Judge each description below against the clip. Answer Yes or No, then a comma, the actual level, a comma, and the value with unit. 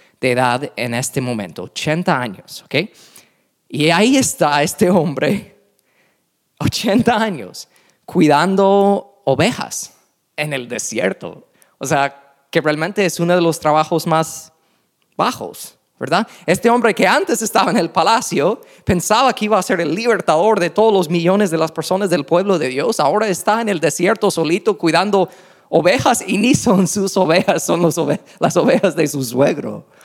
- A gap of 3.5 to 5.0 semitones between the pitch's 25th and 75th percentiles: Yes, average, 4.4 semitones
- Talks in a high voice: No, medium, 175 Hz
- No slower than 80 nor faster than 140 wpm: No, average, 160 wpm